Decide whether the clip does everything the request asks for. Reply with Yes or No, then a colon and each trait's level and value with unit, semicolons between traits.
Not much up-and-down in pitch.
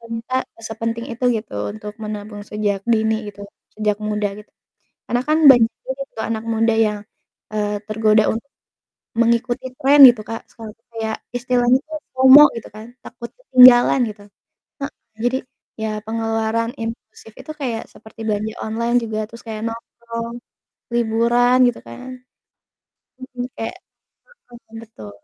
Yes: narrow, 1.9 semitones